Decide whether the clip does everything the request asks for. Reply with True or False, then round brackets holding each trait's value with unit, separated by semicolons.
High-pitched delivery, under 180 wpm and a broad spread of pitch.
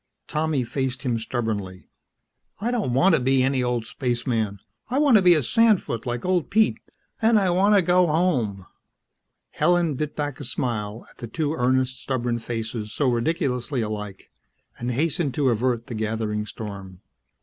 False (130 Hz; 165 wpm; 6.0 semitones)